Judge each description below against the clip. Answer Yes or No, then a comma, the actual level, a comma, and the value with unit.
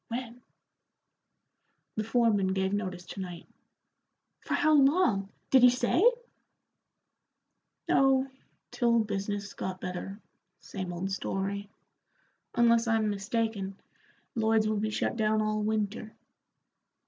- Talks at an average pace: No, slow, 110 wpm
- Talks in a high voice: Yes, high, 215 Hz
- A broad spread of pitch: No, average, 3.1 semitones